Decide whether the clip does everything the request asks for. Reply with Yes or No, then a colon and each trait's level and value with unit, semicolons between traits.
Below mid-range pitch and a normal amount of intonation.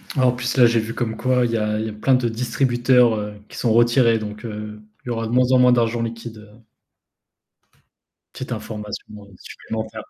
No: low, 115 Hz; narrow, 2.1 semitones